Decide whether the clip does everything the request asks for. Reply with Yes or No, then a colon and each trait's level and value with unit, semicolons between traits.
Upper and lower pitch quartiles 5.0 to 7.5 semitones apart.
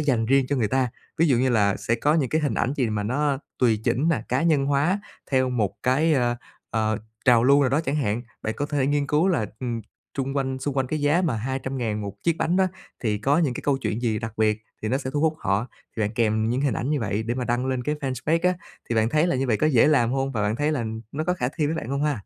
No: average, 4.1 semitones